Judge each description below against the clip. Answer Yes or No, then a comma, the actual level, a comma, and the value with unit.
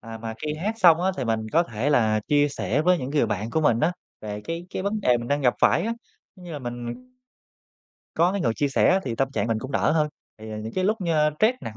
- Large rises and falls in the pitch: Yes, wide, 7.2 semitones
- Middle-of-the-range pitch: Yes, medium, 145 Hz